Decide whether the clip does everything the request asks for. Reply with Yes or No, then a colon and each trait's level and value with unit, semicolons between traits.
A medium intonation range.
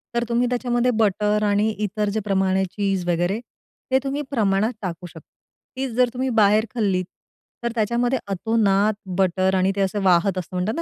Yes: average, 3.6 semitones